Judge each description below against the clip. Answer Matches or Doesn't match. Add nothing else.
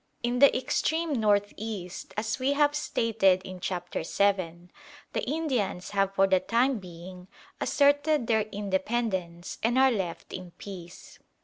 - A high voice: Matches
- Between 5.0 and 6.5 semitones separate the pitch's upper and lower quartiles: Matches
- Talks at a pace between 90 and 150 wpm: Matches